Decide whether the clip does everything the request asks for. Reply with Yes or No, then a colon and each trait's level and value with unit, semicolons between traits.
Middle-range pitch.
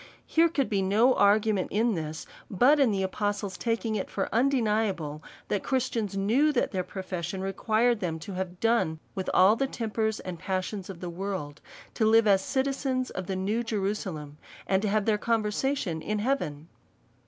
No: high, 205 Hz